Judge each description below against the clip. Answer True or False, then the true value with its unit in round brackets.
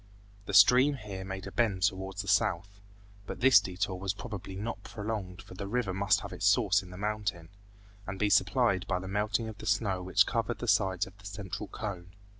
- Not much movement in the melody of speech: True (2.2 semitones)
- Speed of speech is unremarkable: False (210 wpm)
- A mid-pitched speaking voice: False (100 Hz)